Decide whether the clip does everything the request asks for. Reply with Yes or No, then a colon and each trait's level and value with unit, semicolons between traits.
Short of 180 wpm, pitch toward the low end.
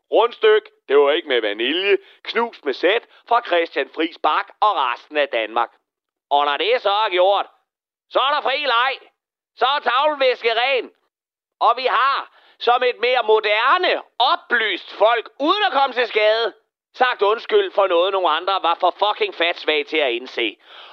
No: average, 170 wpm; high, 240 Hz